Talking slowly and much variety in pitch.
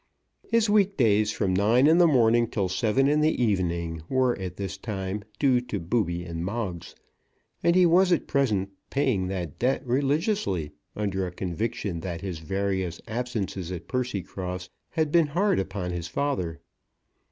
No: average, 155 wpm; wide, 6.7 semitones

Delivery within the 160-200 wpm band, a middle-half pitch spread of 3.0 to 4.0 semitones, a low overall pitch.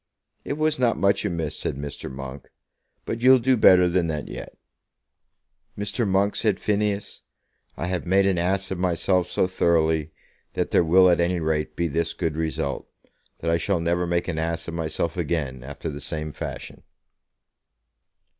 Yes: average, 170 wpm; average, 3.4 semitones; very low, 85 Hz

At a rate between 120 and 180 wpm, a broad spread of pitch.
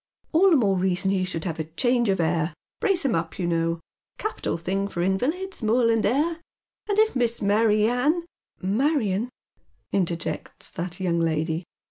Yes: average, 170 wpm; wide, 6.7 semitones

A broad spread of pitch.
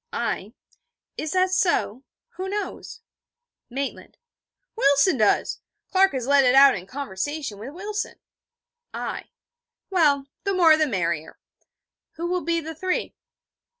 Yes: wide, 5.9 semitones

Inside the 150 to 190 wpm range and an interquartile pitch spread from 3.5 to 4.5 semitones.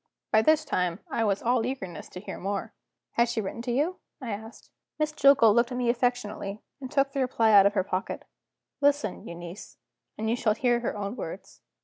No: fast, 205 wpm; average, 3.9 semitones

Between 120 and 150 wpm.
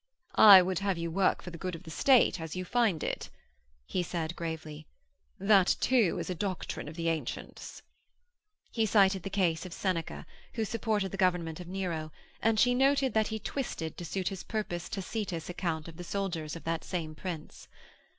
No: average, 190 wpm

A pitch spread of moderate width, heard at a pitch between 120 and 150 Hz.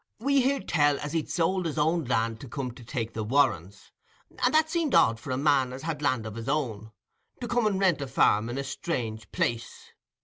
No: wide, 6.7 semitones; medium, 140 Hz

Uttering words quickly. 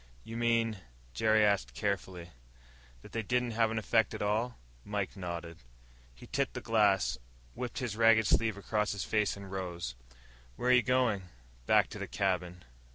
No: average, 165 wpm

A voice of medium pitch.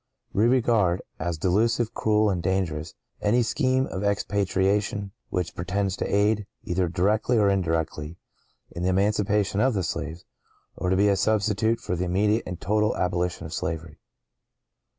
No: low, 100 Hz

